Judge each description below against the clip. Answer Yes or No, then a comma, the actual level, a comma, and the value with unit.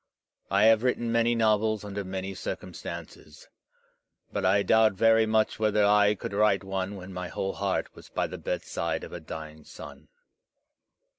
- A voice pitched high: No, low, 100 Hz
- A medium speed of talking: Yes, average, 160 wpm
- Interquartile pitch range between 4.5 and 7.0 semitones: No, narrow, 2.4 semitones